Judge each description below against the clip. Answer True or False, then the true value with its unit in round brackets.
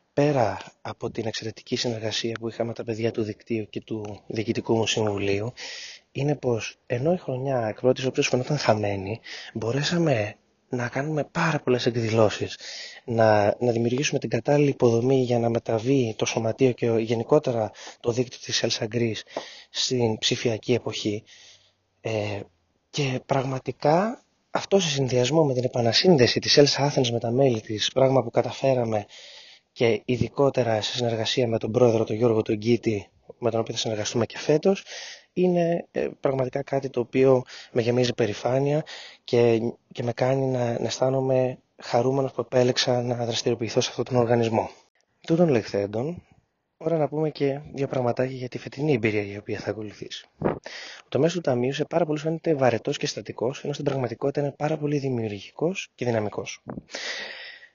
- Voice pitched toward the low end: True (125 Hz)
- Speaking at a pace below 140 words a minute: False (155 wpm)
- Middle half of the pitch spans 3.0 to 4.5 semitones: True (3.5 semitones)